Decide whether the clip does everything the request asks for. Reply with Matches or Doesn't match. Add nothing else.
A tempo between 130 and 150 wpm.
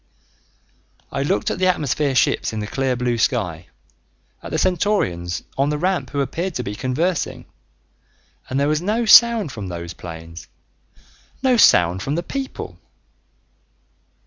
Matches